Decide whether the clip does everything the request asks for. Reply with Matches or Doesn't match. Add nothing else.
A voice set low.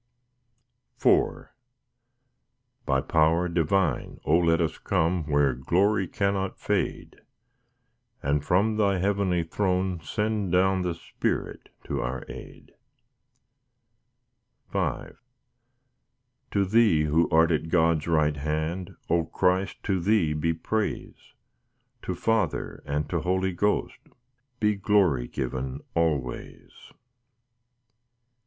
Matches